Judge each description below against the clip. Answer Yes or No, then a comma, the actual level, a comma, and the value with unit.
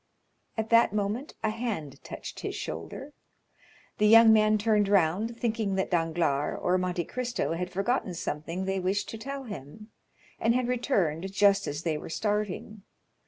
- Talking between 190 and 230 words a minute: No, average, 160 wpm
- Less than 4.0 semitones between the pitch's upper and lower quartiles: No, average, 4.3 semitones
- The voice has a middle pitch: No, high, 205 Hz